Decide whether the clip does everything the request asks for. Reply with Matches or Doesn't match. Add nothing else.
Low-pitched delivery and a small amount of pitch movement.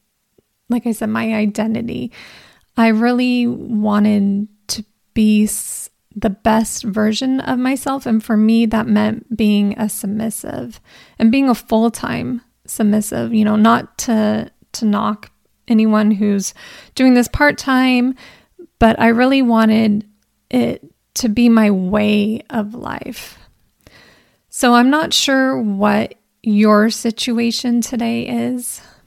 Doesn't match